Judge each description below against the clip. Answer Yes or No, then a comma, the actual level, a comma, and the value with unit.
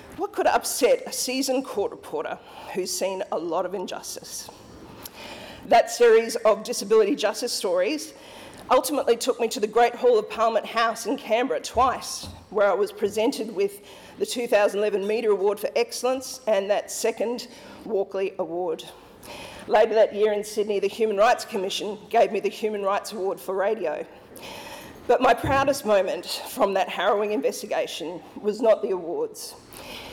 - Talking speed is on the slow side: No, average, 155 wpm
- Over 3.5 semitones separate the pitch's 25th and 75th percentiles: Yes, average, 5.3 semitones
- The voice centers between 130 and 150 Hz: No, high, 230 Hz